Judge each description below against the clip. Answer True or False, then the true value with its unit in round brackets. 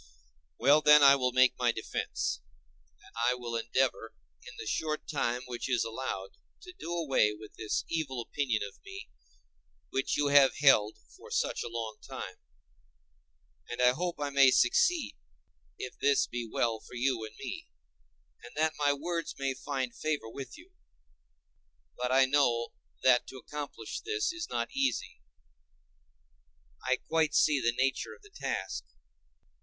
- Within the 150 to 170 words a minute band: True (155 wpm)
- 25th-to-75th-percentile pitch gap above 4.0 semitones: True (4.4 semitones)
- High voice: False (130 Hz)